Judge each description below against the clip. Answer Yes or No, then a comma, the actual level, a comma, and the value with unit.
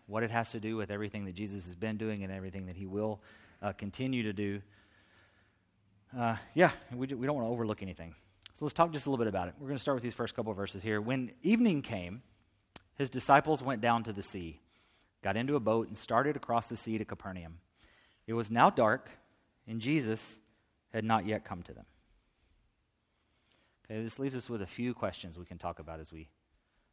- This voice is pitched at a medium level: No, low, 110 Hz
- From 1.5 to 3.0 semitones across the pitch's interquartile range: No, average, 3.4 semitones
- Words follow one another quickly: Yes, fast, 220 wpm